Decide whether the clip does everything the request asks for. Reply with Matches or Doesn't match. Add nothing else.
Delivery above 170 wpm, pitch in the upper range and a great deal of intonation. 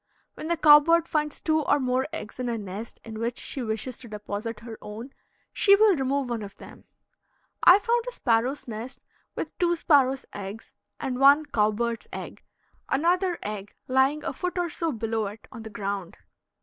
Matches